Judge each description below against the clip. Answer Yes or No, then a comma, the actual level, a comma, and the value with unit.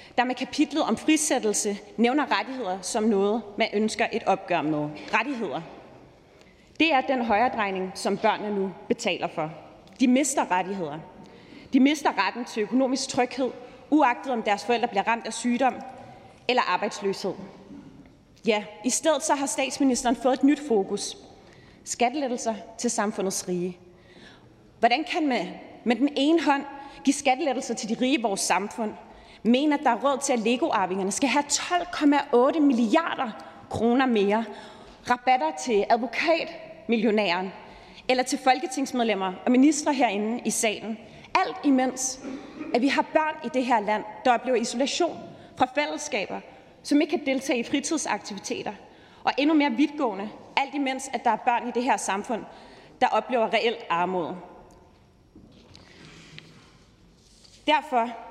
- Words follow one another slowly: Yes, slow, 140 wpm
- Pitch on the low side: No, high, 240 Hz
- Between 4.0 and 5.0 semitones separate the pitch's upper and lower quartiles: Yes, average, 4.5 semitones